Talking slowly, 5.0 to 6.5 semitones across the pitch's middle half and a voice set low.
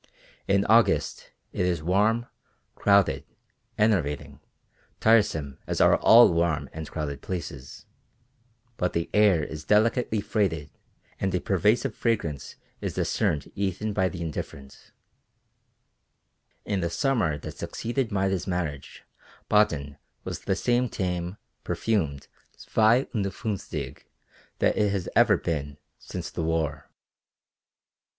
Yes: slow, 115 wpm; wide, 5.4 semitones; very low, 95 Hz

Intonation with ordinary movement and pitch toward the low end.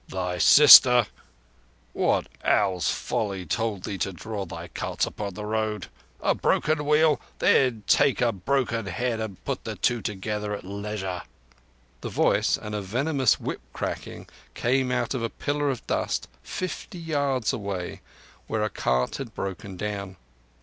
Yes: average, 4.7 semitones; low, 105 Hz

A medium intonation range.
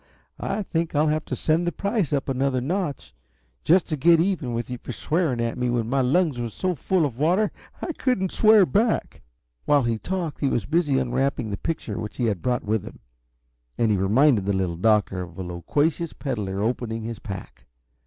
No: wide, 6.9 semitones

